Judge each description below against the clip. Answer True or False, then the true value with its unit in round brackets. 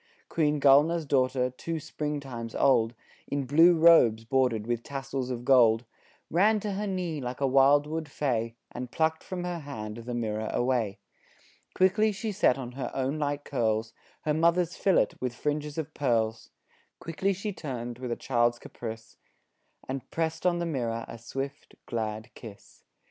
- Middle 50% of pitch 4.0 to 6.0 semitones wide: True (5.2 semitones)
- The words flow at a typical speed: True (160 wpm)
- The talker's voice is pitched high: False (135 Hz)